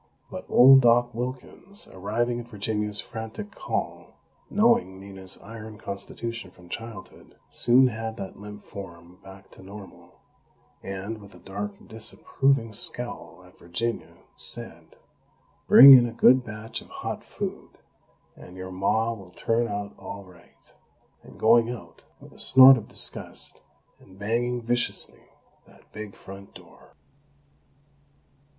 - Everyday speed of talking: No, slow, 130 wpm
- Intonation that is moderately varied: Yes, average, 3.5 semitones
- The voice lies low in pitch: Yes, low, 110 Hz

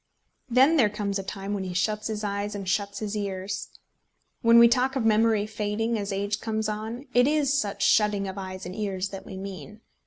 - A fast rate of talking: Yes, fast, 210 wpm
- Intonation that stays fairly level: Yes, narrow, 2.2 semitones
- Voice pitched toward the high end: Yes, high, 210 Hz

